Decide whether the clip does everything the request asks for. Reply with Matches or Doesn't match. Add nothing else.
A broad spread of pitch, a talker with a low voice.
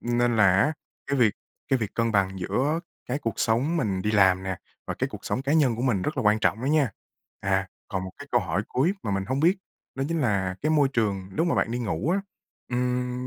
Matches